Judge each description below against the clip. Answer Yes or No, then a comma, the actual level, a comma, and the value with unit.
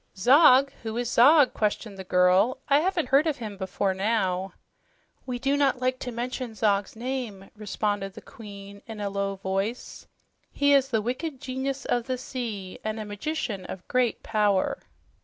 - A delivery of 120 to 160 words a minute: No, average, 170 wpm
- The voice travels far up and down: No, average, 4.4 semitones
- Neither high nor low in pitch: No, high, 225 Hz